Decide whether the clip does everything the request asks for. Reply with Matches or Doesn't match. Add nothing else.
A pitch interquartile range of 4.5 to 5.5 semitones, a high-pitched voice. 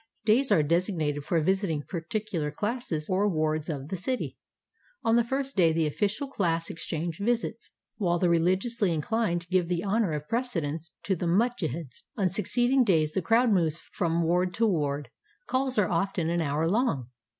Doesn't match